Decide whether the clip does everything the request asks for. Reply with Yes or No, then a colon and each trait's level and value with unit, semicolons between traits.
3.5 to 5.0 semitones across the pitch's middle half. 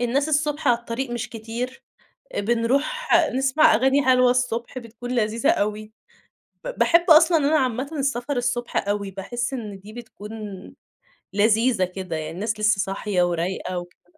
Yes: average, 4.1 semitones